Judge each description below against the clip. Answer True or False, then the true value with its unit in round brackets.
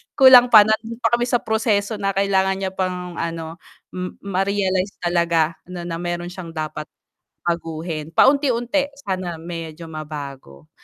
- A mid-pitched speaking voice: True (180 Hz)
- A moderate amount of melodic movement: True (3.6 semitones)